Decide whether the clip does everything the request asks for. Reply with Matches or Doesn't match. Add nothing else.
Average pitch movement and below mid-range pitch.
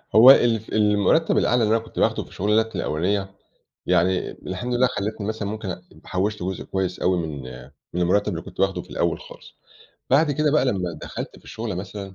Matches